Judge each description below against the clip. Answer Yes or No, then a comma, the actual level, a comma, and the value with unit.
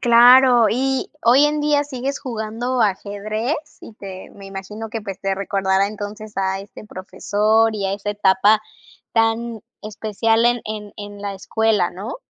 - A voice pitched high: Yes, high, 215 Hz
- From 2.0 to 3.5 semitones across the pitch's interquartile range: Yes, average, 2.8 semitones